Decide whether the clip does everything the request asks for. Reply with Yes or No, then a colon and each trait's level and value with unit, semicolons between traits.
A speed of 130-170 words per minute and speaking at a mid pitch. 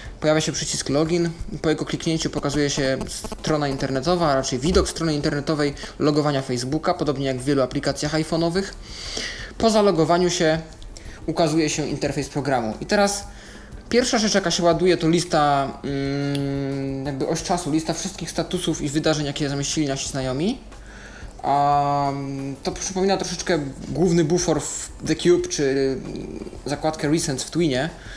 Yes: average, 140 wpm; medium, 155 Hz